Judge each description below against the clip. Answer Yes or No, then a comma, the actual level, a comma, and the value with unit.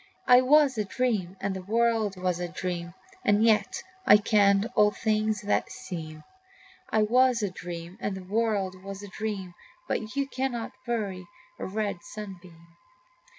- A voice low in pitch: No, high, 205 Hz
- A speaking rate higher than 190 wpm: No, average, 155 wpm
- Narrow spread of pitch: No, average, 3.2 semitones